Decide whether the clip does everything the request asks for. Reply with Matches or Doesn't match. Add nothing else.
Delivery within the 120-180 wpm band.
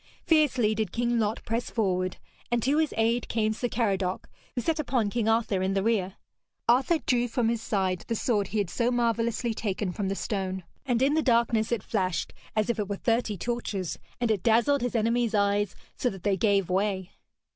Doesn't match